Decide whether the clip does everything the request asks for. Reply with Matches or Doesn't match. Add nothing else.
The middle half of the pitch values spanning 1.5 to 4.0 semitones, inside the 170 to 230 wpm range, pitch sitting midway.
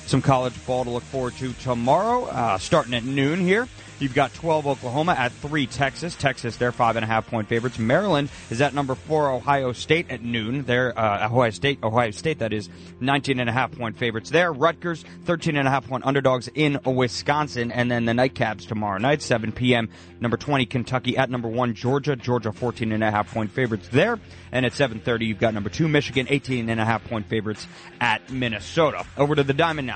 Doesn't match